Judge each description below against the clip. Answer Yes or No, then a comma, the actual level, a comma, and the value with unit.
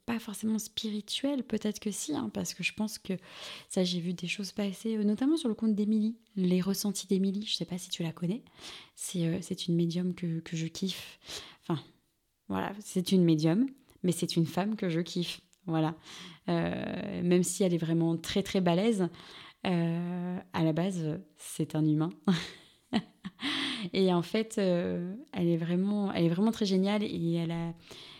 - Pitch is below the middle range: No, medium, 185 Hz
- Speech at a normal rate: Yes, average, 185 wpm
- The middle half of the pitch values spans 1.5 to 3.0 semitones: No, average, 3.7 semitones